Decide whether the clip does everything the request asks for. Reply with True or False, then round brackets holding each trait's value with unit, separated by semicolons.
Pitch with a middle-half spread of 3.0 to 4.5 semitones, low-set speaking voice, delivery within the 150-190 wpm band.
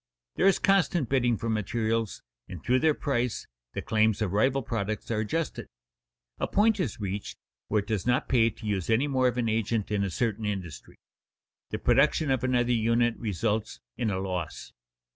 True (3.4 semitones; 115 Hz; 180 wpm)